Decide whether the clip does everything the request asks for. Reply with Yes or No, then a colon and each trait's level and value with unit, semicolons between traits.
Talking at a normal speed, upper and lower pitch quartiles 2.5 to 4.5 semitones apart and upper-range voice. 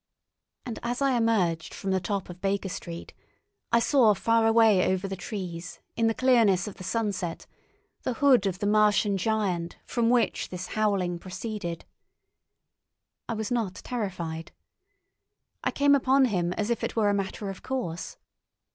Yes: average, 160 wpm; average, 3.9 semitones; high, 205 Hz